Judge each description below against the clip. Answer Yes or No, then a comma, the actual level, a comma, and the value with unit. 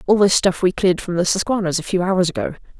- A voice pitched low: No, medium, 180 Hz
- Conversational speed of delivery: No, fast, 260 wpm